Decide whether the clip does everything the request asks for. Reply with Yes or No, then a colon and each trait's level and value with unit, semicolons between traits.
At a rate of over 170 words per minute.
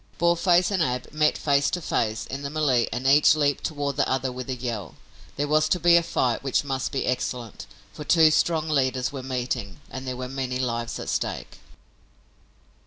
Yes: average, 195 wpm